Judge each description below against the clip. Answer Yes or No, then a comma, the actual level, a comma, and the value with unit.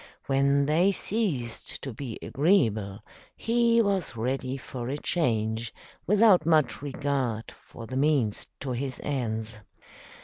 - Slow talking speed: Yes, slow, 125 wpm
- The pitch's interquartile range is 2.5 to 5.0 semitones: No, wide, 5.4 semitones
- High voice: No, low, 135 Hz